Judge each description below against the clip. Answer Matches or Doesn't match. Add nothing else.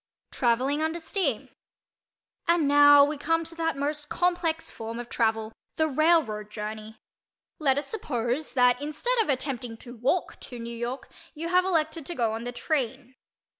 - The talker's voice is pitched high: Matches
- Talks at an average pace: Matches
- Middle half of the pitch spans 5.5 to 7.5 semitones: Doesn't match